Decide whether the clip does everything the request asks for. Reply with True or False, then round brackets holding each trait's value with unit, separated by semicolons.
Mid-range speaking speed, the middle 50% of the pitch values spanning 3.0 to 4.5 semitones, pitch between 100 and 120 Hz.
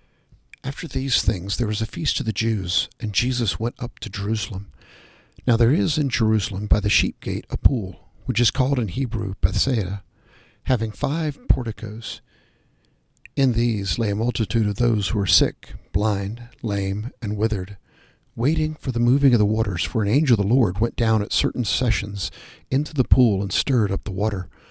True (185 wpm; 3.6 semitones; 115 Hz)